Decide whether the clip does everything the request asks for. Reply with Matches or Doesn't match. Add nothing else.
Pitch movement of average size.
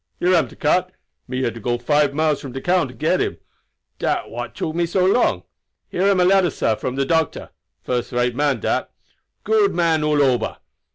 Doesn't match